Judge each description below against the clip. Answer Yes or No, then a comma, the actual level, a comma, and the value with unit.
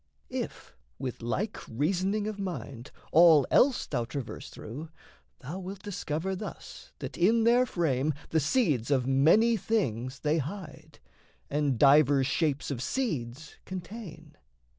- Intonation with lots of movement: Yes, wide, 6.4 semitones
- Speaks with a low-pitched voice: No, medium, 155 Hz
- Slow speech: Yes, slow, 130 wpm